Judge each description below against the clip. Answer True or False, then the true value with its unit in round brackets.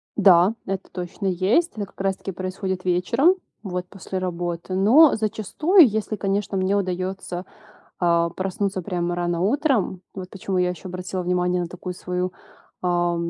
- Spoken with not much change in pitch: True (1.9 semitones)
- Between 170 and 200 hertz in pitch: True (185 Hz)